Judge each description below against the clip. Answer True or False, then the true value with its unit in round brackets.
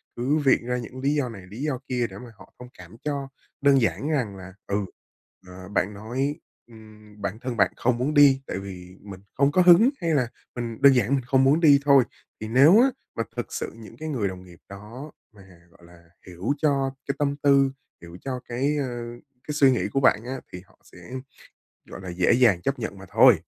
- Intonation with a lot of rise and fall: True (5.7 semitones)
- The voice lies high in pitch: False (125 Hz)